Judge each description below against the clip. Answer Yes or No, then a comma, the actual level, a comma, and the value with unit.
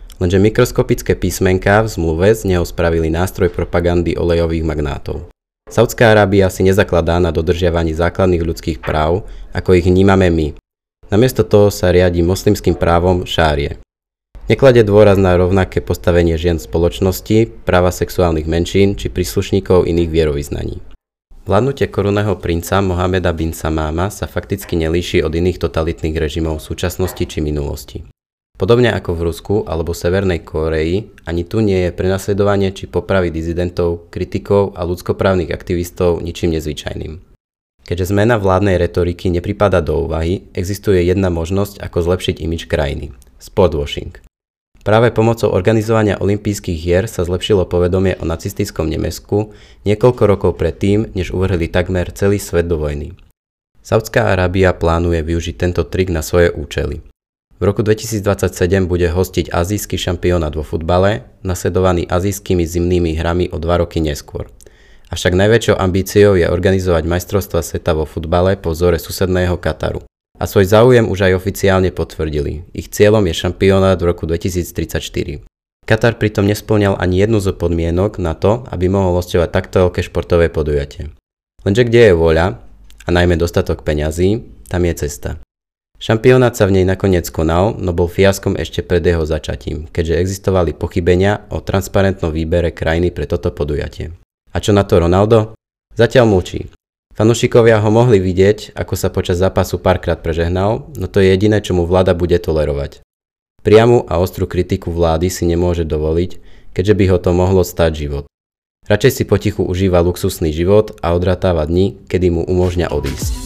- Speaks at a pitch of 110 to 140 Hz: No, very low, 90 Hz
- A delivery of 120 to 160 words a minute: Yes, average, 145 wpm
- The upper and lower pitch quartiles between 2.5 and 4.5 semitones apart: Yes, average, 2.8 semitones